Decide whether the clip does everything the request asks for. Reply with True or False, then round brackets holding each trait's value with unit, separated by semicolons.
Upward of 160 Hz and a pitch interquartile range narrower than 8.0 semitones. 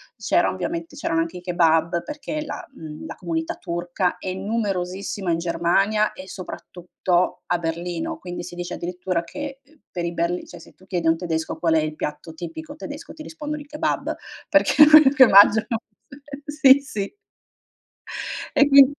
False (185 Hz; 8.4 semitones)